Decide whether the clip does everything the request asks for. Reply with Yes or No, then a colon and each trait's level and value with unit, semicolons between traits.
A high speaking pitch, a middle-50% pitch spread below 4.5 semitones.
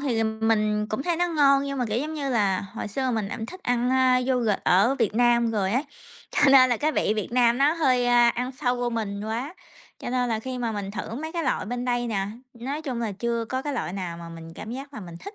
Yes: high, 245 Hz; average, 3.5 semitones